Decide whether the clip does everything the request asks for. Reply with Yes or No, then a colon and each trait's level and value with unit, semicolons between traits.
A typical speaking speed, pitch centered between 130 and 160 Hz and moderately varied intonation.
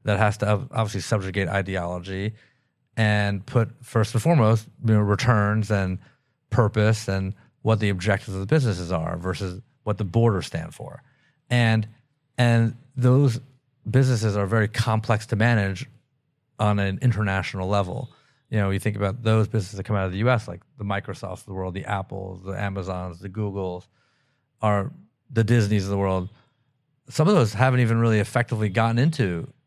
No: average, 170 wpm; low, 110 Hz; average, 4.0 semitones